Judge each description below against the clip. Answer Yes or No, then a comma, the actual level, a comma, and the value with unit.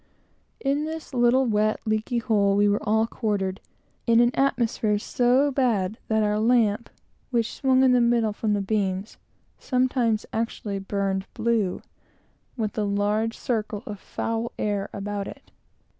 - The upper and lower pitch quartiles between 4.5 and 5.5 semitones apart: No, average, 2.7 semitones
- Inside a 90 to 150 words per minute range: Yes, average, 145 wpm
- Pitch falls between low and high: No, high, 220 Hz